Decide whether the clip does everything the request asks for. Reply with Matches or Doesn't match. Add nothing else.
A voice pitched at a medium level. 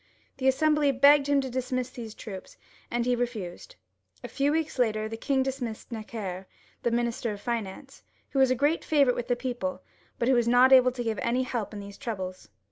Doesn't match